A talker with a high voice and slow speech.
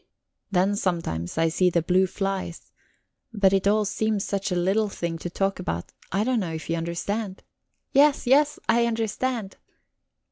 No: high, 195 Hz; average, 165 wpm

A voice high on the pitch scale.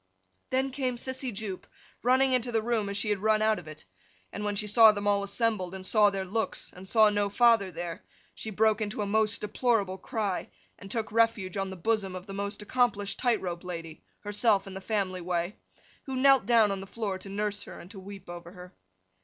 Yes: high, 205 Hz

